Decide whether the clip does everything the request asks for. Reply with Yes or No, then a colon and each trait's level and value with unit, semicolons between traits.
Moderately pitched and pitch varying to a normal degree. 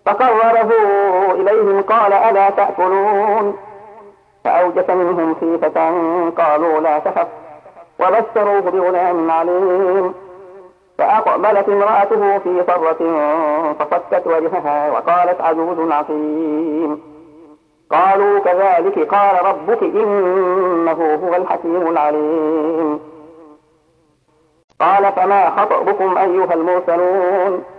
Yes: medium, 180 Hz; average, 3.6 semitones